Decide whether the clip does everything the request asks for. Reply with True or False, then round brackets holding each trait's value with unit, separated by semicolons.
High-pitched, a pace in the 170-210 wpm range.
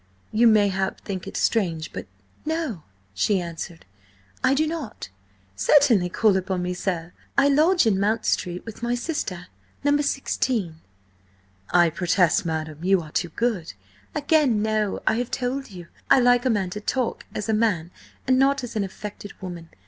False (210 Hz; 160 wpm)